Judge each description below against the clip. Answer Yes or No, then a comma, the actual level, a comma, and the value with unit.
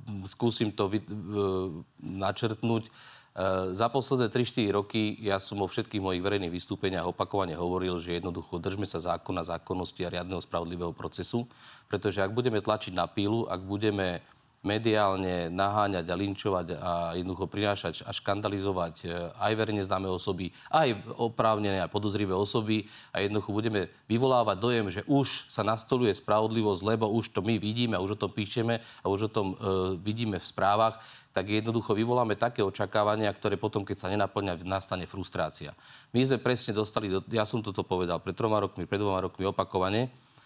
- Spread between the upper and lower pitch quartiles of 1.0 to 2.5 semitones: No, average, 2.9 semitones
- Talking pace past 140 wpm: Yes, average, 160 wpm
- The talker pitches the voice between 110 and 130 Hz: No, low, 100 Hz